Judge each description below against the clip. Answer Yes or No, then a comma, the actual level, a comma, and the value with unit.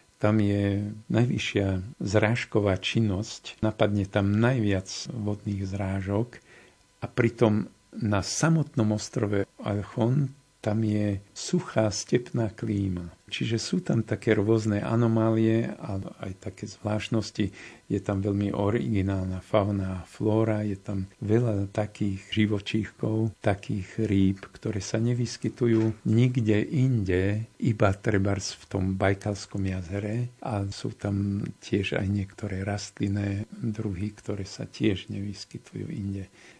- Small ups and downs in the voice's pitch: Yes, narrow, 2.1 semitones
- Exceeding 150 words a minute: No, slow, 110 wpm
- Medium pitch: No, low, 105 Hz